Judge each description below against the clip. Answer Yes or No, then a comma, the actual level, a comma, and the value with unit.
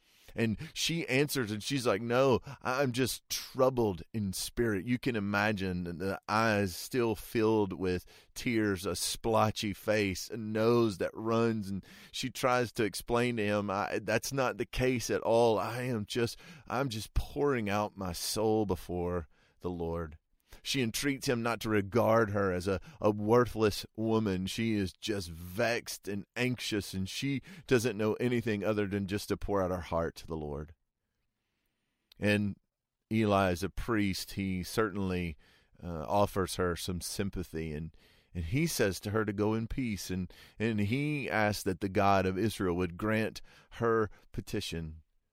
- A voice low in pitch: Yes, low, 105 Hz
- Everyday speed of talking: Yes, average, 165 wpm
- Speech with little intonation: No, average, 3.6 semitones